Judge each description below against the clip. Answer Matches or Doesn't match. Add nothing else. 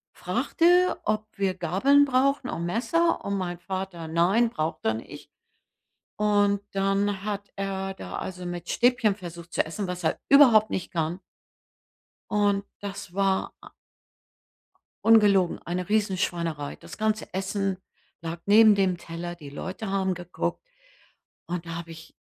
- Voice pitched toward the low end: Doesn't match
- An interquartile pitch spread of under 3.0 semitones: Doesn't match